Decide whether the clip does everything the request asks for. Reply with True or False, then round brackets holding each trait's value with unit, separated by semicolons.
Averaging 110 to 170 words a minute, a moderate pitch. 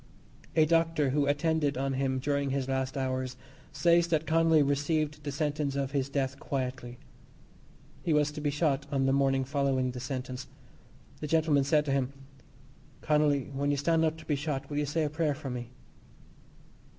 False (180 wpm; 145 Hz)